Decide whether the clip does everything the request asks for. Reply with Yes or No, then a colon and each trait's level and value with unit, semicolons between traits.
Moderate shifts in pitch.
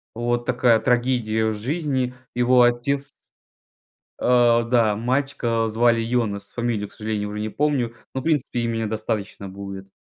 No: narrow, 2.3 semitones